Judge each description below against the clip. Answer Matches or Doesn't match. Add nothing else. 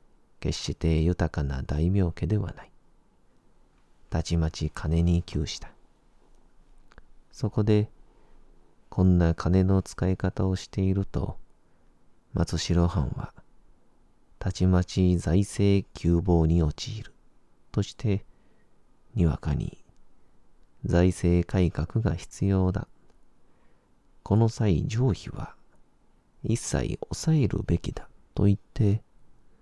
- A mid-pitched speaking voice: Doesn't match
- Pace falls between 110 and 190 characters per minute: Matches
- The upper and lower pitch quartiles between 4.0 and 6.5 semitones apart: Doesn't match